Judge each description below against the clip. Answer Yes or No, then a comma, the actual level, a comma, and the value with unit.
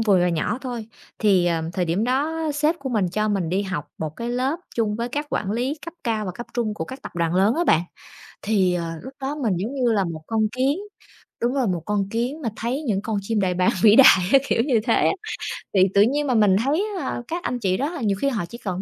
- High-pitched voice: Yes, high, 225 Hz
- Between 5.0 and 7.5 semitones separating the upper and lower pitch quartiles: Yes, wide, 5.5 semitones